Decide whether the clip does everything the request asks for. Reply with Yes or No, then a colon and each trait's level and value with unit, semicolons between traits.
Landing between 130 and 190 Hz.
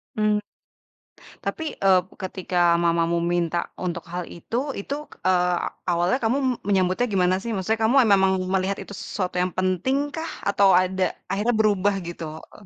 Yes: medium, 185 Hz